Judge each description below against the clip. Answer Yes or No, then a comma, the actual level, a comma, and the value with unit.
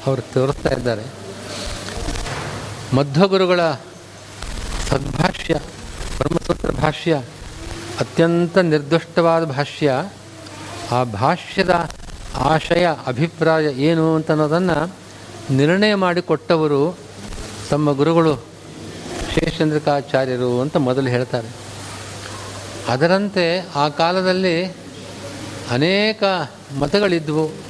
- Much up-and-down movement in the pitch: Yes, wide, 6.7 semitones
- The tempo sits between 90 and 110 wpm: No, slow, 65 wpm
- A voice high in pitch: No, medium, 145 Hz